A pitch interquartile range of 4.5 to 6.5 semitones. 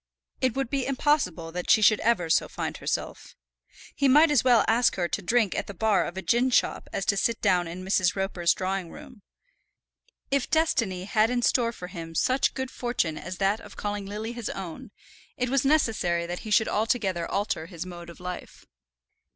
Yes: average, 5.3 semitones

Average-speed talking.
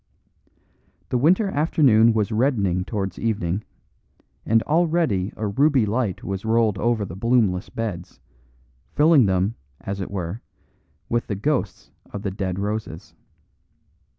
No: slow, 125 wpm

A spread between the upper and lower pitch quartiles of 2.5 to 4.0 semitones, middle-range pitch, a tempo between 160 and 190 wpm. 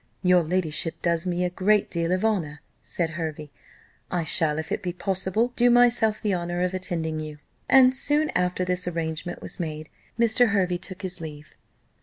Yes: average, 3.6 semitones; medium, 180 Hz; average, 180 wpm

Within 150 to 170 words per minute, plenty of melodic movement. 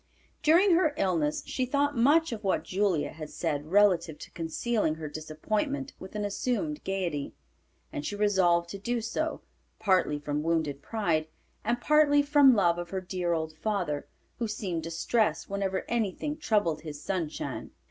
Yes: average, 160 wpm; wide, 6.7 semitones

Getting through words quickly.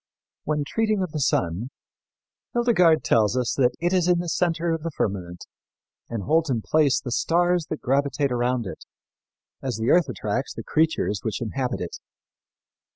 No: average, 165 wpm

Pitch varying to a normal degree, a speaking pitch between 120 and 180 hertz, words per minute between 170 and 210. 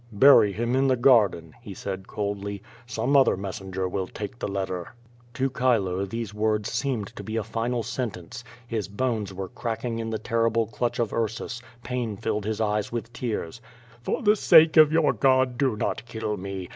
No: average, 3.5 semitones; low, 110 Hz; average, 185 wpm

